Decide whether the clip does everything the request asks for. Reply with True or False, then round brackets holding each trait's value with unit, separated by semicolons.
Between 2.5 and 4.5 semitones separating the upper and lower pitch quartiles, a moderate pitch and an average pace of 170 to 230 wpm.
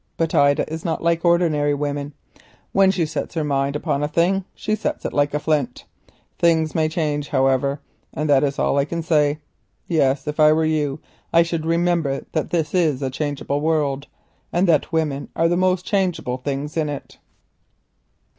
True (2.8 semitones; 155 Hz; 180 wpm)